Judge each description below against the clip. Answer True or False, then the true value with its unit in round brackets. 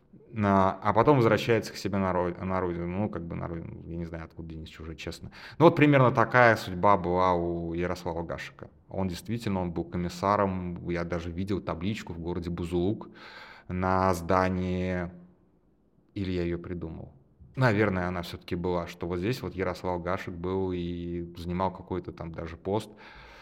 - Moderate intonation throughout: False (2.2 semitones)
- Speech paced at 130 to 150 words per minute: False (160 wpm)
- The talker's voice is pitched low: True (90 Hz)